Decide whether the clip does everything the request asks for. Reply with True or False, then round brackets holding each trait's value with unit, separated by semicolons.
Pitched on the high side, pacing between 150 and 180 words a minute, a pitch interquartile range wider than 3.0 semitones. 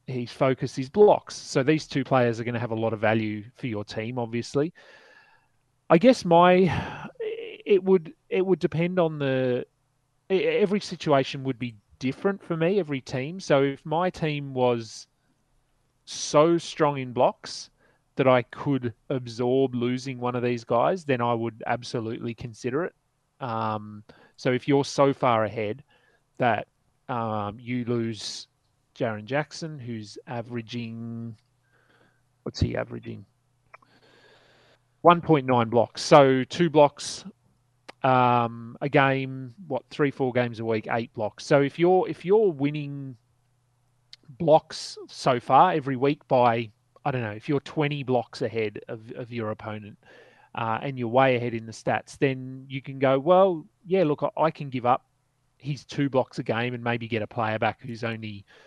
False (130 Hz; 160 wpm; 3.7 semitones)